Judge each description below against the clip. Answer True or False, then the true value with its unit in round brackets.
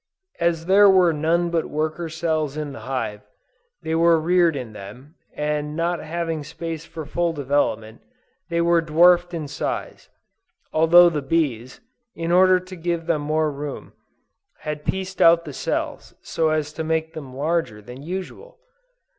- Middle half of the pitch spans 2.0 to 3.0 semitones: True (2.5 semitones)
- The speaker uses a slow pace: False (155 wpm)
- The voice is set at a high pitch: False (160 Hz)